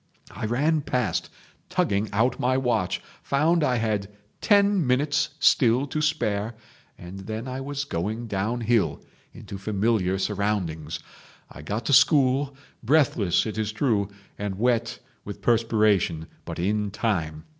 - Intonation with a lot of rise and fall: No, average, 4.6 semitones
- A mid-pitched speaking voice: No, low, 110 Hz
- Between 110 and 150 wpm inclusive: Yes, slow, 135 wpm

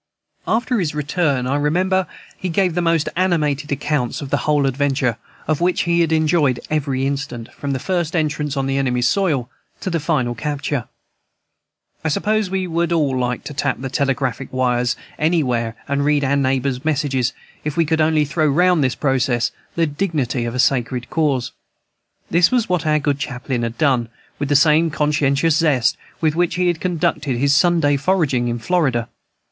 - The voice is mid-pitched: Yes, medium, 145 Hz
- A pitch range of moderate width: Yes, average, 3.8 semitones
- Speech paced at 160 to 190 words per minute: Yes, average, 180 wpm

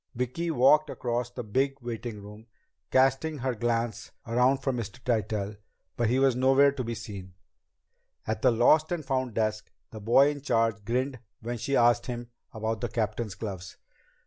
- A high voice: No, low, 120 Hz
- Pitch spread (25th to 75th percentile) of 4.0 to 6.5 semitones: No, average, 3.2 semitones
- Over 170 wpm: No, average, 165 wpm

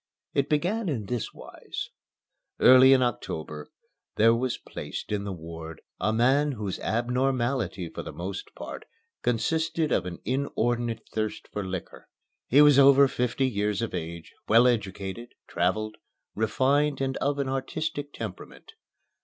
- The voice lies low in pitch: Yes, low, 120 Hz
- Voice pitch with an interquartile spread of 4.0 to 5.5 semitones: Yes, average, 5.0 semitones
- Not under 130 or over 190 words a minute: Yes, average, 140 wpm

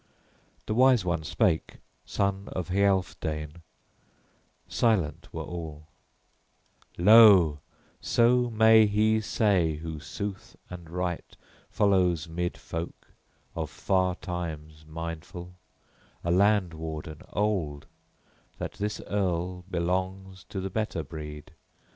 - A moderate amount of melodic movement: Yes, average, 3.8 semitones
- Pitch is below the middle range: Yes, very low, 90 Hz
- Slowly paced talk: Yes, slow, 105 wpm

